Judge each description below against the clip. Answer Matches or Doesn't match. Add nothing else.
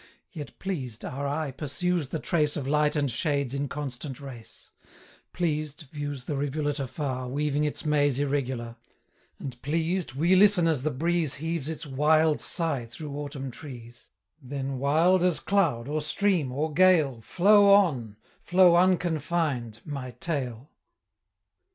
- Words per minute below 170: Matches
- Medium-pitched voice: Matches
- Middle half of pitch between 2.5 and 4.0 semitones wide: Matches